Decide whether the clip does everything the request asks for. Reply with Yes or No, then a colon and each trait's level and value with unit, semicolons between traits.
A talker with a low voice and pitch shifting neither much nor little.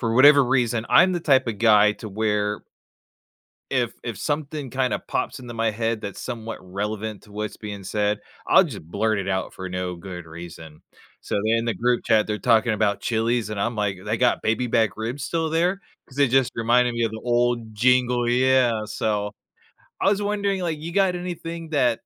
Yes: low, 115 Hz; average, 3.6 semitones